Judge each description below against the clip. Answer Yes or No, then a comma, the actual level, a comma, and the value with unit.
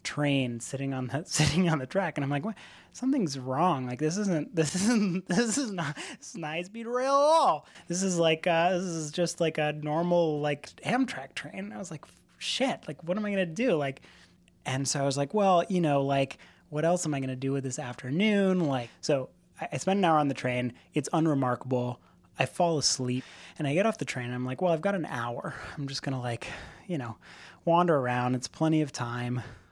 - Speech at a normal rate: No, fast, 230 wpm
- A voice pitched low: No, medium, 155 Hz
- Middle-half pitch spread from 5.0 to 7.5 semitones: Yes, wide, 5.6 semitones